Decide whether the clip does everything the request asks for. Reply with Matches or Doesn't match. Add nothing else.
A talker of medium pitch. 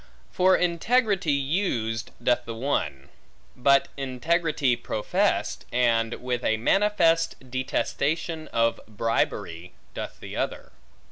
Doesn't match